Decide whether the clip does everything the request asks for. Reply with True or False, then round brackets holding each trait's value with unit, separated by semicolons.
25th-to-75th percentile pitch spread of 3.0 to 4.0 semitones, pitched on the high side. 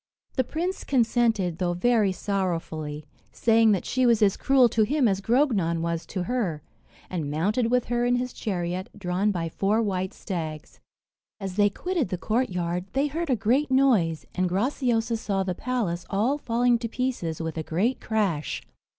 False (5.5 semitones; 210 Hz)